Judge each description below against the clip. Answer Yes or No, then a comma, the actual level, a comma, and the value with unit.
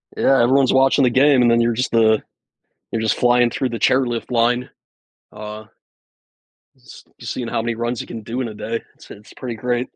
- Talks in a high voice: No, low, 120 Hz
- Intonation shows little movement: Yes, narrow, 1.7 semitones